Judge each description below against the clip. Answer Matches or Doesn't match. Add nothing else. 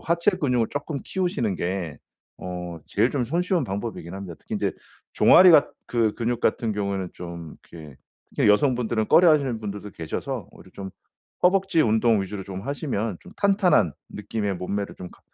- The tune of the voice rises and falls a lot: Matches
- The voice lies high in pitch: Doesn't match